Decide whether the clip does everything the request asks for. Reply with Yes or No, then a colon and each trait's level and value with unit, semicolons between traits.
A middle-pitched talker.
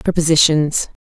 Yes: medium, 160 Hz